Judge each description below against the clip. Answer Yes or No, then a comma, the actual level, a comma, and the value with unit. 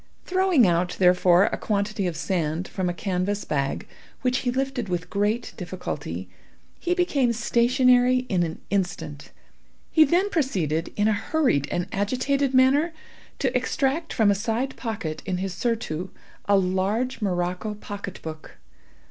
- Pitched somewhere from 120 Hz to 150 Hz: No, high, 205 Hz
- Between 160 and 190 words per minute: No, average, 145 wpm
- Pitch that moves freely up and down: Yes, wide, 6.1 semitones